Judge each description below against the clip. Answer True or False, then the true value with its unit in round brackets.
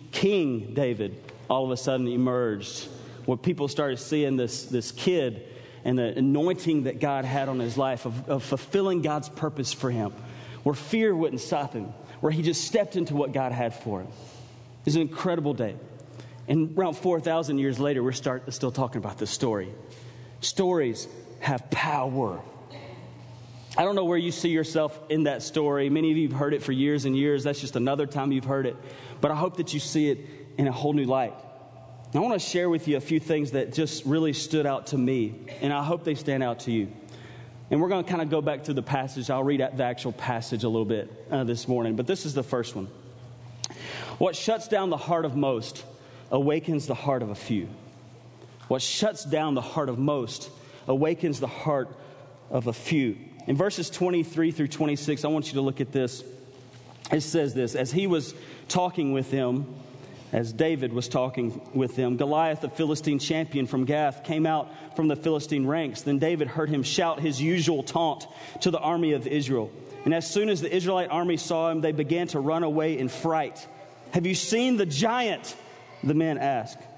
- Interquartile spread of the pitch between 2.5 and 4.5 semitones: True (3.8 semitones)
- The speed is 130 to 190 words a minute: False (205 wpm)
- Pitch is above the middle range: False (140 Hz)